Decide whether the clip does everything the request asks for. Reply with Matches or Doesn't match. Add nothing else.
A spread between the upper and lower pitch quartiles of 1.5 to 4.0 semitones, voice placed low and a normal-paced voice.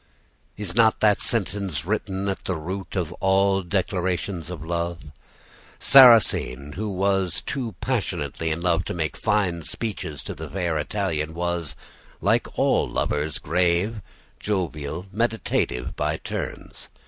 Doesn't match